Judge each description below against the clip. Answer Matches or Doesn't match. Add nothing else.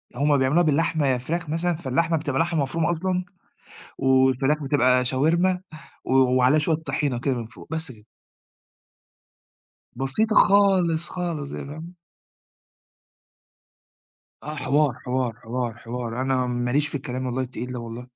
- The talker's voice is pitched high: Doesn't match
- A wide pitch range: Doesn't match